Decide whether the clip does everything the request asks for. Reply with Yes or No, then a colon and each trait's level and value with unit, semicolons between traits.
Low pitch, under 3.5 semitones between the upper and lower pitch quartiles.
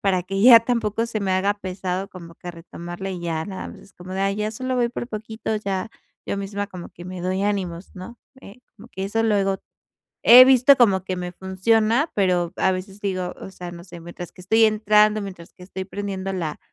No: high, 195 Hz; average, 2.7 semitones